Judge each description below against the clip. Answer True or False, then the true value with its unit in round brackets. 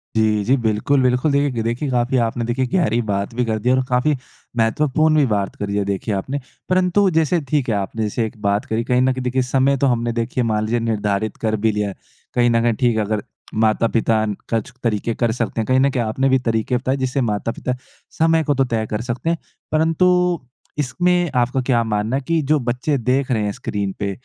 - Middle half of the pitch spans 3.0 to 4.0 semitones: True (3.6 semitones)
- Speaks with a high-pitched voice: False (120 Hz)